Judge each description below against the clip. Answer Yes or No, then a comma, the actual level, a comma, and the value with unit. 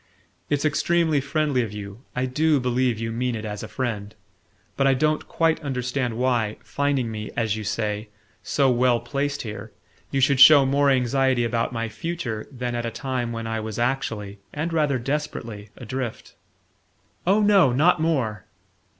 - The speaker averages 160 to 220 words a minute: Yes, average, 165 wpm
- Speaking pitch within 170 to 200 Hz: No, low, 125 Hz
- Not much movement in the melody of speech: No, average, 3.9 semitones